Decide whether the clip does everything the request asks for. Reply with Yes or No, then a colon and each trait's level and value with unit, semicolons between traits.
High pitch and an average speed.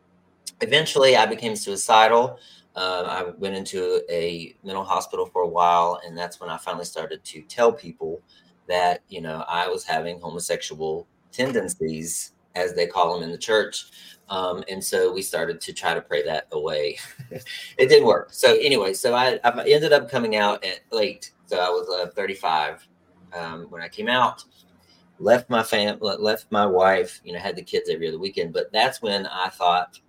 No: medium, 140 Hz; average, 185 wpm